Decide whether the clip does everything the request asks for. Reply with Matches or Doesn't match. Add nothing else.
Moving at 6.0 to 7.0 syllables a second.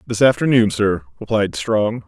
Doesn't match